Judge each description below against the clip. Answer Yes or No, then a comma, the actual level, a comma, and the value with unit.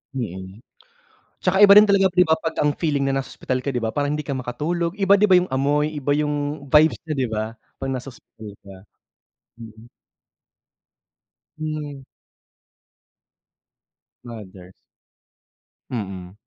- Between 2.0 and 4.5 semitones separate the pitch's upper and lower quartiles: No, average, 5.2 semitones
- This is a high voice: No, medium, 145 Hz